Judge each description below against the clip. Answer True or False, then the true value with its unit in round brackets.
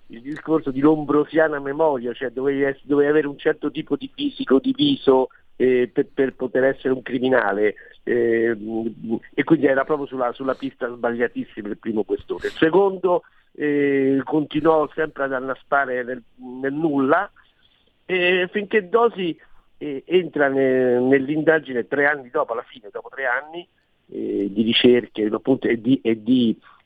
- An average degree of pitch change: True (3.7 semitones)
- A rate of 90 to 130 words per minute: False (155 wpm)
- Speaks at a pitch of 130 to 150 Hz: True (140 Hz)